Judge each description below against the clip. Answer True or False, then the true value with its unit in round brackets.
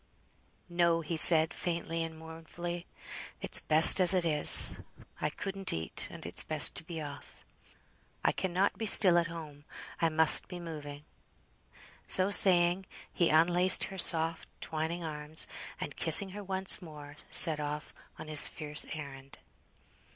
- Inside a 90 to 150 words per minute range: True (145 wpm)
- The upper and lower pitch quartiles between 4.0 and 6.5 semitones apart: False (2.4 semitones)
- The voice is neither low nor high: True (165 Hz)